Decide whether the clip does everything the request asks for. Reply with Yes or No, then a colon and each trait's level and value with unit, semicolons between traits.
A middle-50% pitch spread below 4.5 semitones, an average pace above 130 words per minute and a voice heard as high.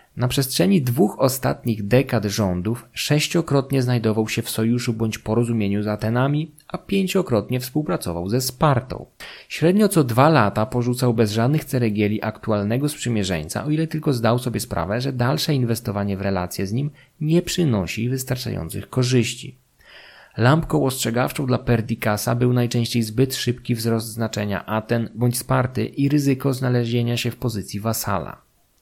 No: average, 3.6 semitones; average, 140 wpm; low, 120 Hz